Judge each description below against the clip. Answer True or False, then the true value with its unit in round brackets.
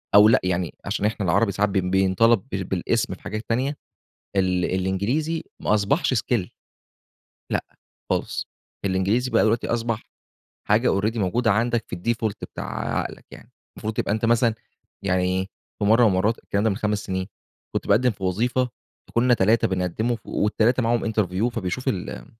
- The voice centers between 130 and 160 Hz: False (105 Hz)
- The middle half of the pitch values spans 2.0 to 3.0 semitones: False (3.7 semitones)